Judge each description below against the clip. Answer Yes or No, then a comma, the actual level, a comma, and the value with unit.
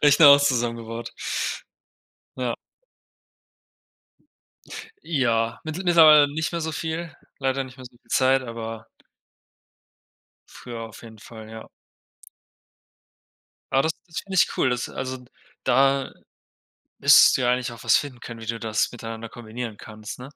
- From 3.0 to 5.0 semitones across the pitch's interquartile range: Yes, average, 3.7 semitones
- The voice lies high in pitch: No, low, 125 Hz